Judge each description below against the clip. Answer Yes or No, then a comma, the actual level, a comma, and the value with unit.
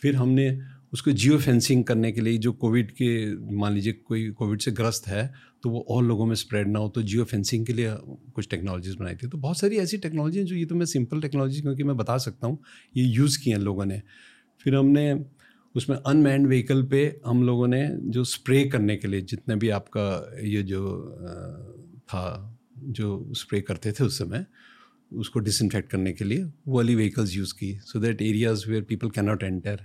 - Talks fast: Yes, fast, 200 wpm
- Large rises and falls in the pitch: No, average, 4.2 semitones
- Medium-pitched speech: No, low, 120 Hz